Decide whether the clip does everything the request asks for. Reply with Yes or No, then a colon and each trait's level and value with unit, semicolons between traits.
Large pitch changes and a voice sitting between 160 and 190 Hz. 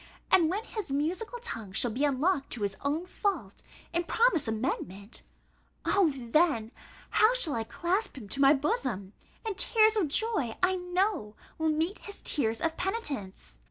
No: wide, 8.5 semitones; very high, 315 Hz